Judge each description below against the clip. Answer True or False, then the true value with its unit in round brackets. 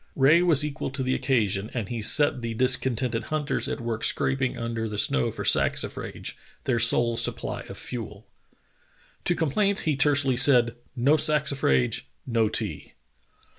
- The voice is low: True (125 Hz)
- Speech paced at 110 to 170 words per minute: True (150 wpm)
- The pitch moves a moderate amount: True (3.7 semitones)